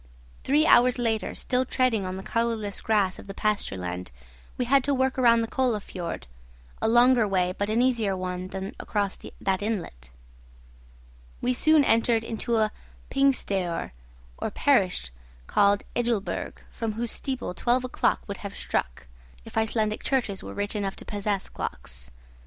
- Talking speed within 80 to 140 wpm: No, average, 160 wpm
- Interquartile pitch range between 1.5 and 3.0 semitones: No, average, 4.0 semitones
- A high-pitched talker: Yes, high, 215 Hz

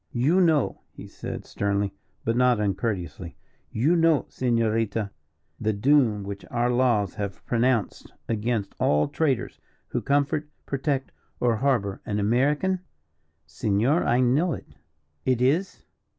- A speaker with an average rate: No, slow, 125 wpm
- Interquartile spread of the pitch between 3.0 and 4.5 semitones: No, average, 5.2 semitones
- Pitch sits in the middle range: No, low, 120 Hz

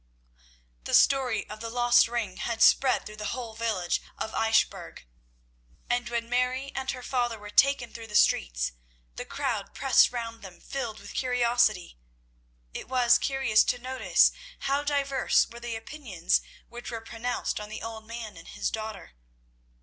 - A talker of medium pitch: No, high, 235 Hz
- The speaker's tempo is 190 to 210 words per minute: No, average, 160 wpm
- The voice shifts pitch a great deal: No, narrow, 2.4 semitones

